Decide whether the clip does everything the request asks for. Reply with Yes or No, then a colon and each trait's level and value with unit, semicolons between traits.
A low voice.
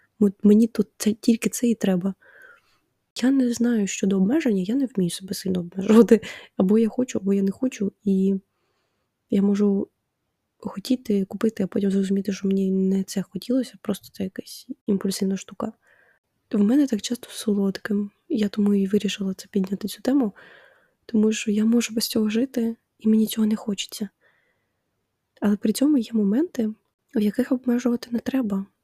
No: high, 210 Hz